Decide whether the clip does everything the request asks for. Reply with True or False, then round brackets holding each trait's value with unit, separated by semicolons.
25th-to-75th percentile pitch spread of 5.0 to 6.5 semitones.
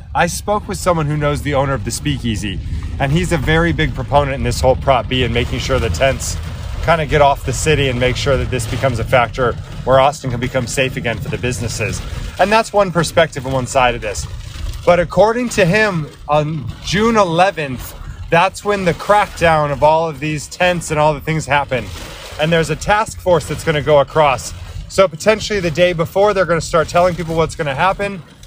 True (5.3 semitones)